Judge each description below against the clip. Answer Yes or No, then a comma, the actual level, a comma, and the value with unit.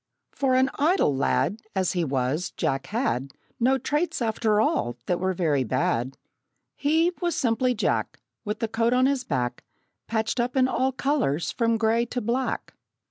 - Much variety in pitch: Yes, wide, 7.6 semitones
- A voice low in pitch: No, high, 225 Hz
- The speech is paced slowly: No, average, 165 wpm